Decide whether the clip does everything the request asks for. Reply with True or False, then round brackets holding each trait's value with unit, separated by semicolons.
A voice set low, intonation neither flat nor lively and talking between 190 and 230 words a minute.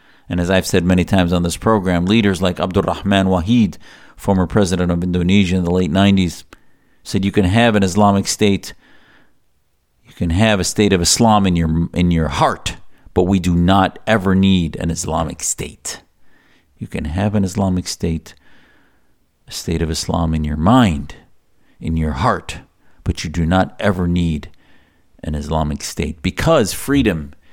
False (90 Hz; 3.0 semitones; 165 wpm)